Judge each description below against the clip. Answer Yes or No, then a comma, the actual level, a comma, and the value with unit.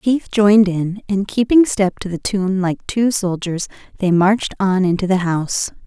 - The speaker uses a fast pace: No, average, 185 wpm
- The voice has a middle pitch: No, high, 195 Hz